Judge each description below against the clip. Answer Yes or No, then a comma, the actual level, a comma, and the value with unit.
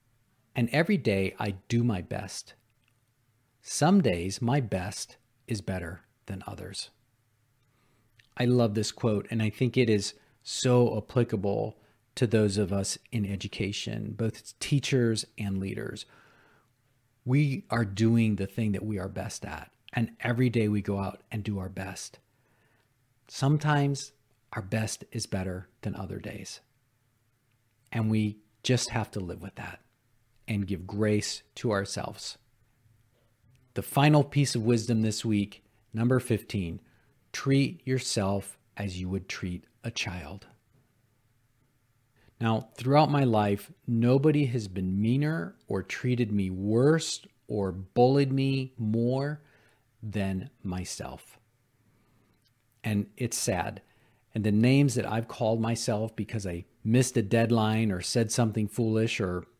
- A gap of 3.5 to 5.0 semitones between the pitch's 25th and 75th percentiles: No, average, 2.9 semitones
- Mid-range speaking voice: No, low, 115 Hz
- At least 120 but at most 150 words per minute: Yes, slow, 135 wpm